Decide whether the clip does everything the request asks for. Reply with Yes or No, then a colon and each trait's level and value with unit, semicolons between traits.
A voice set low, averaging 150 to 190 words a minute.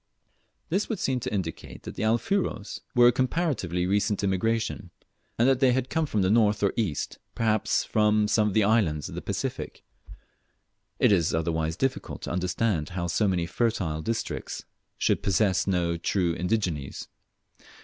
Yes: low, 105 Hz; average, 160 wpm